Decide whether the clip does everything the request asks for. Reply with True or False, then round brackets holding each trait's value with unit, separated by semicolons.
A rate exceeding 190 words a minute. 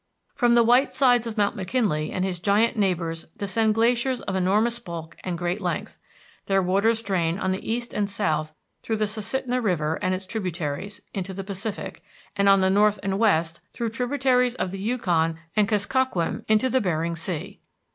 False (175 wpm)